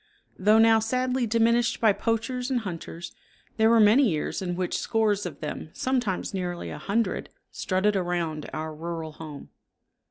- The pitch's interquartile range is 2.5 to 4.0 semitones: No, average, 4.8 semitones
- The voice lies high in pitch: Yes, high, 205 Hz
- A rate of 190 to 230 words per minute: No, average, 155 wpm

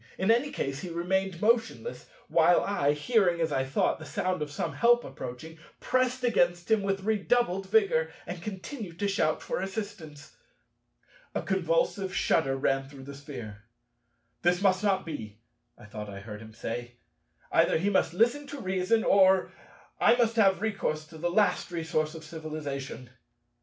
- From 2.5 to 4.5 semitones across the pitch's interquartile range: No, wide, 5.5 semitones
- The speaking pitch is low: No, medium, 175 Hz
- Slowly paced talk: No, average, 165 wpm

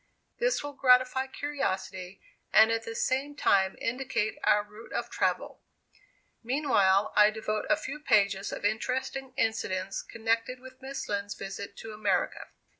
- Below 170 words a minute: Yes, average, 140 wpm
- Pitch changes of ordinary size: Yes, average, 4.5 semitones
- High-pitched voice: Yes, high, 225 Hz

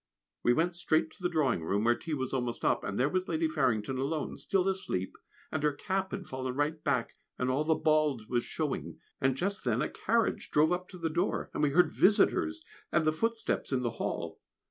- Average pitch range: No, wide, 5.9 semitones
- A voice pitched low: No, medium, 155 Hz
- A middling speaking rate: No, fast, 215 wpm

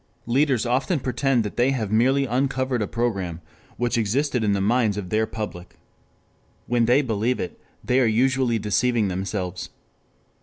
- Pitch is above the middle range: No, low, 120 Hz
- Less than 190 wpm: Yes, average, 160 wpm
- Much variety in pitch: No, average, 3.6 semitones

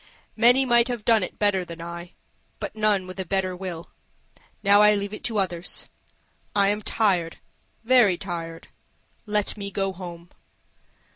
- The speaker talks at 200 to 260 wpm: No, average, 155 wpm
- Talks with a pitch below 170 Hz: No, high, 195 Hz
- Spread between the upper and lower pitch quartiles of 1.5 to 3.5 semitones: Yes, average, 3.0 semitones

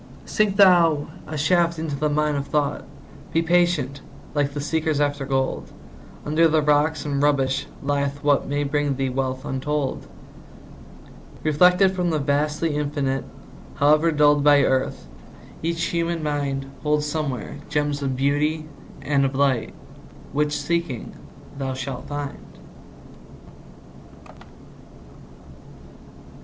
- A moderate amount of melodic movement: No, narrow, 2.0 semitones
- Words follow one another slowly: Yes, slow, 120 wpm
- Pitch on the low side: No, medium, 145 Hz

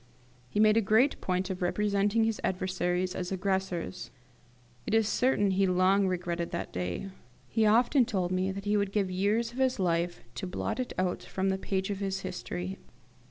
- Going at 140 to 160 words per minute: No, average, 190 wpm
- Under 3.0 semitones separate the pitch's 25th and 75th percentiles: Yes, narrow, 2.4 semitones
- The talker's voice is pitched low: No, high, 190 Hz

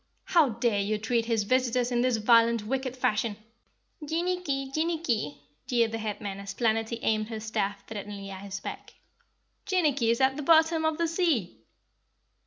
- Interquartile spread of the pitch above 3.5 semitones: Yes, average, 4.6 semitones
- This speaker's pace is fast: No, average, 160 wpm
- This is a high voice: Yes, high, 235 Hz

